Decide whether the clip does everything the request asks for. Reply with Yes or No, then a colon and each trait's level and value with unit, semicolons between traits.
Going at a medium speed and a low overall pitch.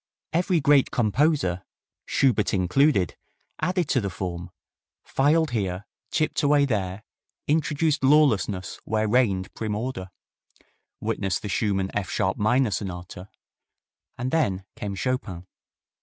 No: slow, 115 wpm; low, 110 Hz